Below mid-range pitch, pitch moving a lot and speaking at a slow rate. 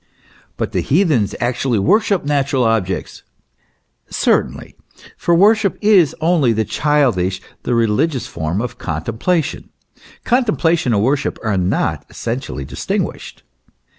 Yes: low, 130 Hz; wide, 7.7 semitones; slow, 125 wpm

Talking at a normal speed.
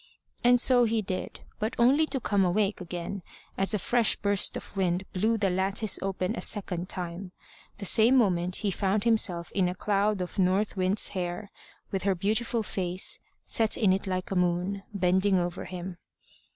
Yes: average, 180 wpm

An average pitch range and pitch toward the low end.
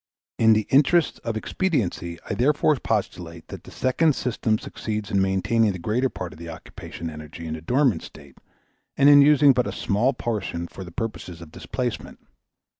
No: wide, 6.9 semitones; low, 110 Hz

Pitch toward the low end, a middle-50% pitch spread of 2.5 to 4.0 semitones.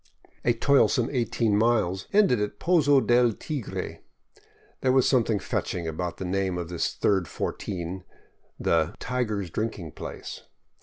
No: low, 105 Hz; wide, 5.5 semitones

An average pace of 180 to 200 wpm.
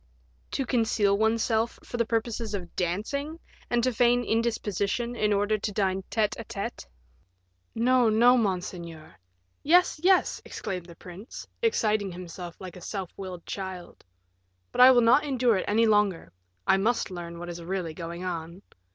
No: average, 160 wpm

